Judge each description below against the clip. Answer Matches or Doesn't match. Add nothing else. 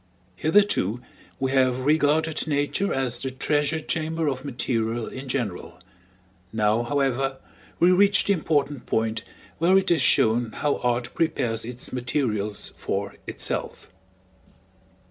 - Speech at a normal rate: Doesn't match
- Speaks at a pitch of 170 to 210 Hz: Doesn't match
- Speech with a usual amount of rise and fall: Matches